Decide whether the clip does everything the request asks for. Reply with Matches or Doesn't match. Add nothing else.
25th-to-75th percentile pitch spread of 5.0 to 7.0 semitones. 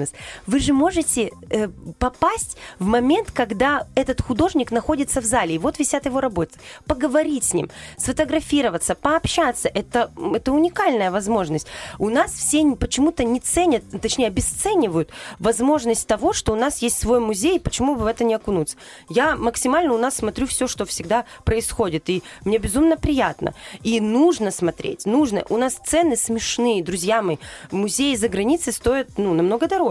Matches